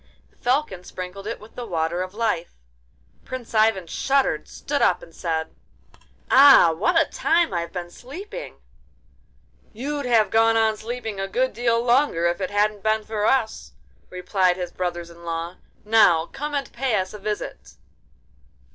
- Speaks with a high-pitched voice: Yes, high, 210 Hz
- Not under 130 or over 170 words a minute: Yes, average, 155 wpm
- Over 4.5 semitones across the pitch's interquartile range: Yes, wide, 5.6 semitones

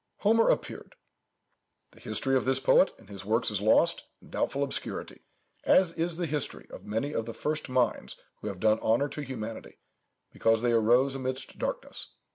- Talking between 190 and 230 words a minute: No, average, 175 wpm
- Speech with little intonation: No, average, 4.4 semitones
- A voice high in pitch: No, low, 130 Hz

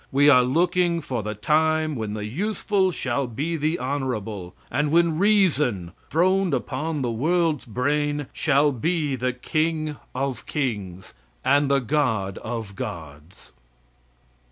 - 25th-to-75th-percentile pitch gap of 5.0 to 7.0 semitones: Yes, wide, 5.6 semitones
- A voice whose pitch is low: No, medium, 145 Hz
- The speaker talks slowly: Yes, slow, 130 wpm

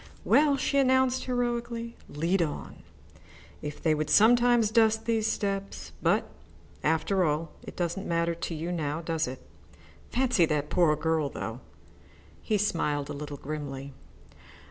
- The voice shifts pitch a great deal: Yes, wide, 7.2 semitones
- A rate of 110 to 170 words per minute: Yes, average, 140 wpm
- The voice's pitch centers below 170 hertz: No, medium, 175 Hz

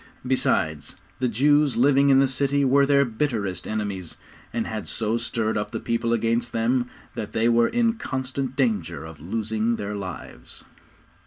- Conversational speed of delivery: Yes, average, 160 wpm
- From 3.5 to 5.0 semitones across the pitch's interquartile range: Yes, average, 3.9 semitones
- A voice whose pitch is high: No, low, 115 Hz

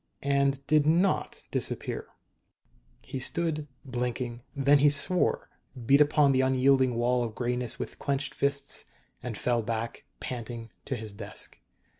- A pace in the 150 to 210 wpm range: No, slow, 135 wpm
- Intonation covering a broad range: No, average, 2.8 semitones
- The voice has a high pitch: No, low, 130 Hz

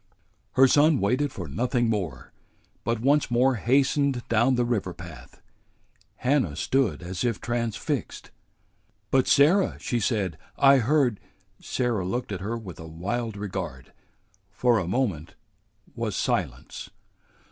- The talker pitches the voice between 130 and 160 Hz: No, low, 115 Hz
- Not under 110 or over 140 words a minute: Yes, slow, 135 wpm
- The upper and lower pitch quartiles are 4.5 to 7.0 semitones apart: Yes, average, 5.2 semitones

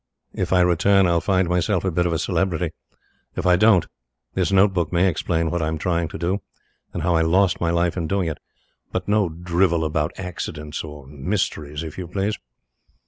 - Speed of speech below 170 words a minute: No, average, 200 wpm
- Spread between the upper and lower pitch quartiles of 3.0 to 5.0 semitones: No, narrow, 2.5 semitones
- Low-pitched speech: Yes, very low, 85 Hz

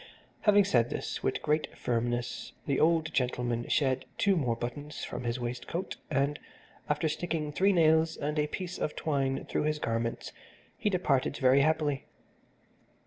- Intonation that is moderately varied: Yes, average, 4.2 semitones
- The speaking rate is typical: Yes, average, 150 wpm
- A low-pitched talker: No, medium, 150 Hz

